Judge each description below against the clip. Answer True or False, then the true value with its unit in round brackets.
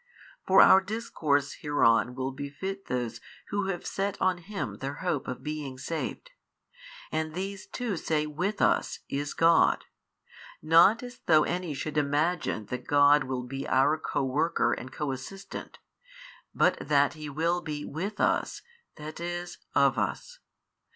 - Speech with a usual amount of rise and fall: True (4.5 semitones)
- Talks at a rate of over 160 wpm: False (150 wpm)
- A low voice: False (155 Hz)